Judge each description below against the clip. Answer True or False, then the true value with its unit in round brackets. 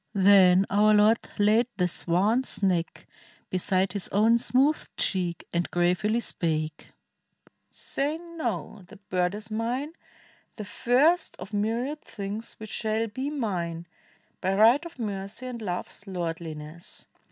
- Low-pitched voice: False (210 Hz)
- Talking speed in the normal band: False (130 wpm)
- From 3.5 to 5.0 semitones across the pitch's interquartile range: True (4.5 semitones)